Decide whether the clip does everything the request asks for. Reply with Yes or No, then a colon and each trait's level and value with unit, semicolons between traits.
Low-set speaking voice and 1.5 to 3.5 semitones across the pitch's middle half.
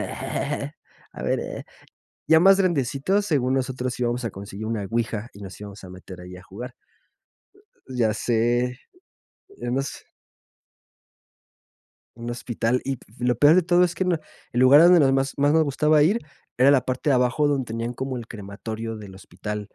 No: low, 125 Hz; average, 4.3 semitones